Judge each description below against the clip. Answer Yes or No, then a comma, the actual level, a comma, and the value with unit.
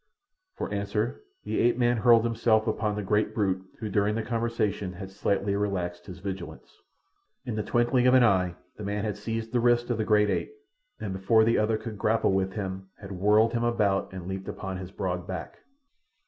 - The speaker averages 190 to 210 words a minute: Yes, average, 200 wpm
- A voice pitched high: No, low, 105 Hz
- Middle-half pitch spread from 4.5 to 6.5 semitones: No, average, 3.0 semitones